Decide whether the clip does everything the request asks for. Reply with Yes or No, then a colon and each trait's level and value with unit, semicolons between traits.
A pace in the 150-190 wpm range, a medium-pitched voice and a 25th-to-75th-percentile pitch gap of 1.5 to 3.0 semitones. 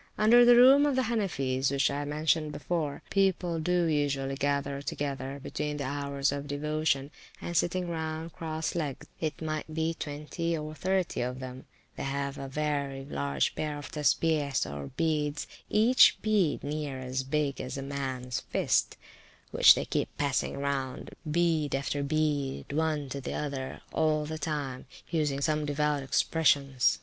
Yes: average, 160 wpm; medium, 145 Hz; narrow, 2.5 semitones